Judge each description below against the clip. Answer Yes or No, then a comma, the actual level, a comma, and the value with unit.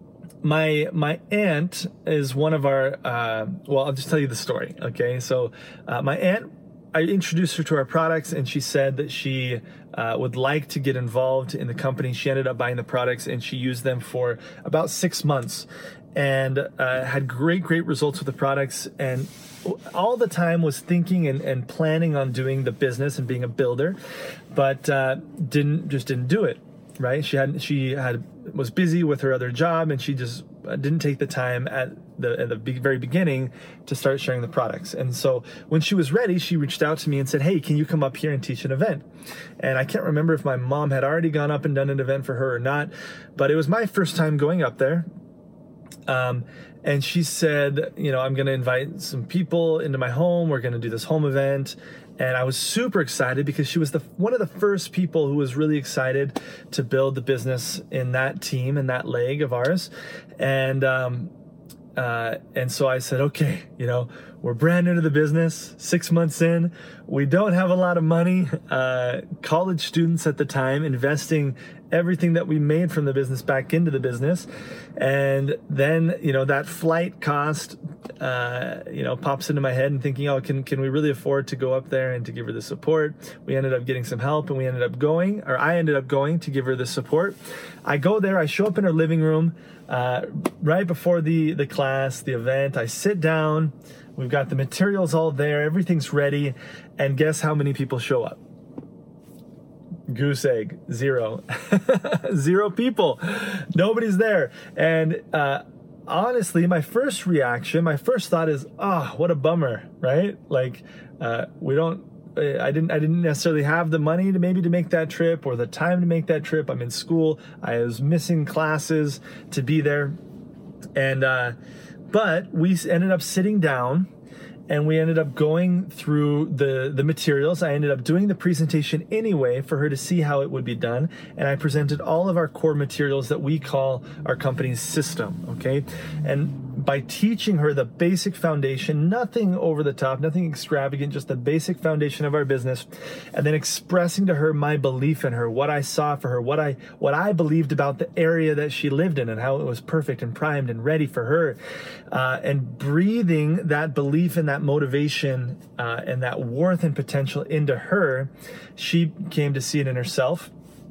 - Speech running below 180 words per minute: No, average, 200 wpm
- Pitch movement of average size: Yes, average, 3.6 semitones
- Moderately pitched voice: Yes, medium, 150 Hz